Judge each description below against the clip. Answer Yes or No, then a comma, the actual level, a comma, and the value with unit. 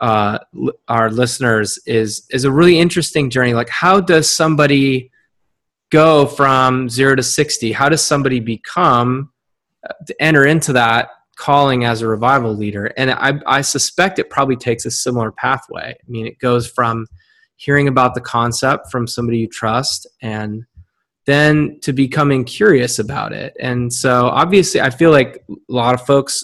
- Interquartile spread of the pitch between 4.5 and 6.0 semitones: No, average, 3.4 semitones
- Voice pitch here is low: Yes, low, 130 Hz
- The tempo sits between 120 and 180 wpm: Yes, average, 165 wpm